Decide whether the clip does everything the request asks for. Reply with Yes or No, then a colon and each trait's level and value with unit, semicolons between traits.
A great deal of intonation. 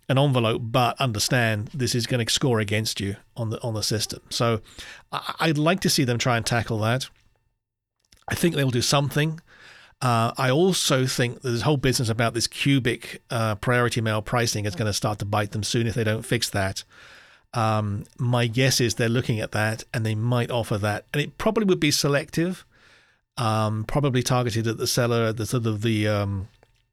No: average, 2.9 semitones